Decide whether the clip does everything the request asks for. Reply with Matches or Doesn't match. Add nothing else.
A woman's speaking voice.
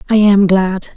Matches